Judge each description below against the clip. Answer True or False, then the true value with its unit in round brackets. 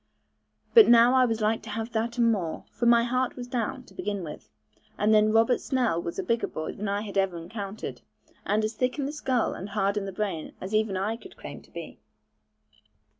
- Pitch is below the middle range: False (220 Hz)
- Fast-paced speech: True (225 wpm)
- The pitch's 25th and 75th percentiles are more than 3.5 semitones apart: False (3.2 semitones)